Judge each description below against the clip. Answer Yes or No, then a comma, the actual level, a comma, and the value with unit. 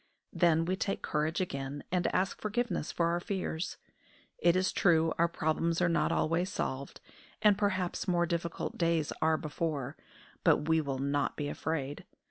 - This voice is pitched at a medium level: Yes, medium, 165 Hz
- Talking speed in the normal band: Yes, average, 160 wpm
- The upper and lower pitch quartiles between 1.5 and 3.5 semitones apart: Yes, average, 2.8 semitones